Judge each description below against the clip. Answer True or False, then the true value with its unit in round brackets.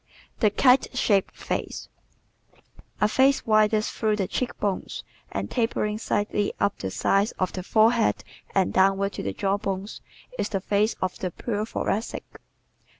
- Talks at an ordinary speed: True (155 wpm)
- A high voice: True (205 Hz)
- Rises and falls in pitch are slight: True (2.0 semitones)